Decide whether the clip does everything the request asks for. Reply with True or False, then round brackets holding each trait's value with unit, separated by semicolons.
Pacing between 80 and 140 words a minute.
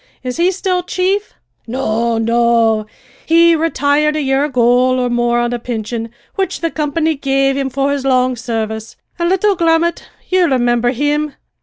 False (160 wpm)